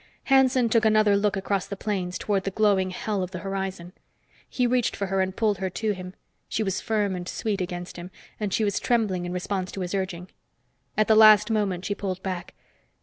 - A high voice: Yes, high, 195 Hz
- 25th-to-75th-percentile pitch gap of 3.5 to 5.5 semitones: No, narrow, 2.5 semitones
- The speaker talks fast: Yes, fast, 210 wpm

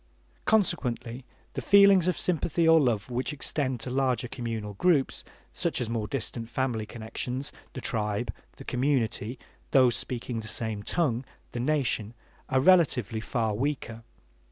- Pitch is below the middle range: Yes, low, 125 Hz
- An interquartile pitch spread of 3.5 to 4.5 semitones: Yes, average, 4.0 semitones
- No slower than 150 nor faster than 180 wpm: No, average, 140 wpm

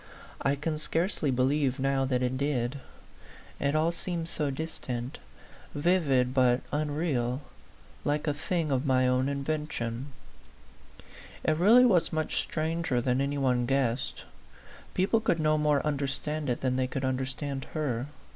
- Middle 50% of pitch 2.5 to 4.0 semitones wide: Yes, average, 3.1 semitones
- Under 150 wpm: Yes, average, 140 wpm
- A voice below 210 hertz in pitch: Yes, medium, 140 Hz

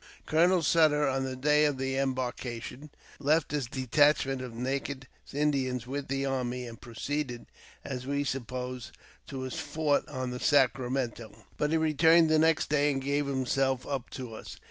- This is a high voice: No, low, 135 Hz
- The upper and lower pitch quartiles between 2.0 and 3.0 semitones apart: Yes, narrow, 2.6 semitones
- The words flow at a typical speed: Yes, average, 165 wpm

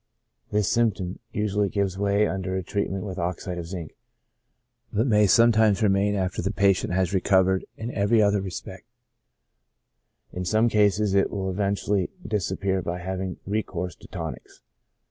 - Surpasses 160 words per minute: No, average, 145 wpm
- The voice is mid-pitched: No, low, 100 Hz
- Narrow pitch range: Yes, narrow, 1.9 semitones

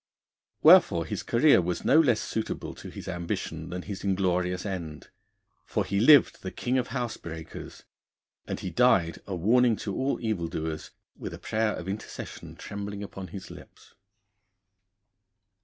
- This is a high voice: No, very low, 95 Hz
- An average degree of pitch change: Yes, average, 4.3 semitones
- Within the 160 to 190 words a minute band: No, average, 145 wpm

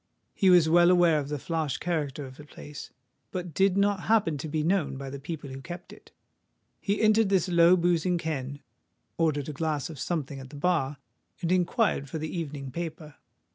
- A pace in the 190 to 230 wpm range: Yes, average, 195 wpm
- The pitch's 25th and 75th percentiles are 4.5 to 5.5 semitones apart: No, average, 3.7 semitones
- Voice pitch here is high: No, medium, 160 Hz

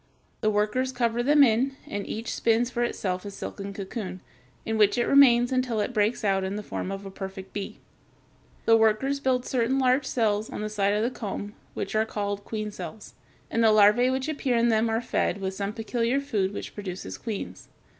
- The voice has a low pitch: No, high, 220 Hz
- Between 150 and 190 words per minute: No, fast, 205 wpm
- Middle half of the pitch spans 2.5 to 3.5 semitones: Yes, average, 3.2 semitones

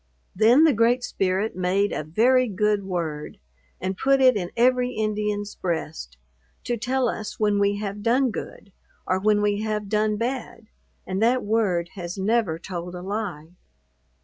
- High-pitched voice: Yes, high, 210 Hz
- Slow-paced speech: No, average, 160 wpm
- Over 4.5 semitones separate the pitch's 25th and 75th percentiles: No, average, 3.6 semitones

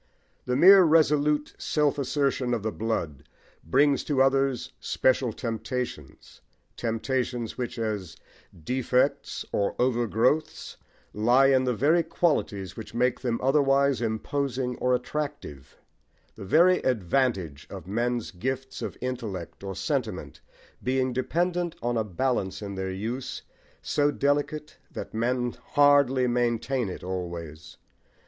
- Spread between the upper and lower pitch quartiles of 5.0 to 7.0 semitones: No, average, 4.0 semitones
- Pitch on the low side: Yes, low, 125 Hz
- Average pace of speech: No, slow, 125 wpm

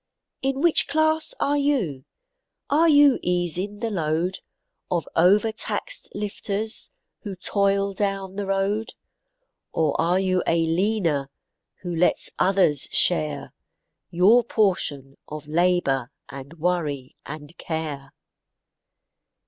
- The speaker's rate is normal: No, slow, 110 wpm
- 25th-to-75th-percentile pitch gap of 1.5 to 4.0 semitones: No, average, 4.8 semitones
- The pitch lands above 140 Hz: Yes, medium, 185 Hz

